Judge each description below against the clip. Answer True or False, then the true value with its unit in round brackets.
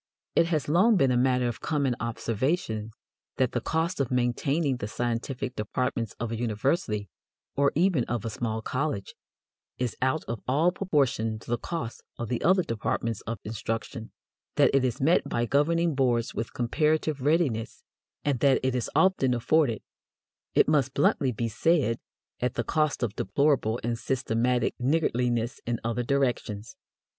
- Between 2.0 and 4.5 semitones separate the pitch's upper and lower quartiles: True (4.1 semitones)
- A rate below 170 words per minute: True (160 wpm)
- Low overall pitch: True (125 Hz)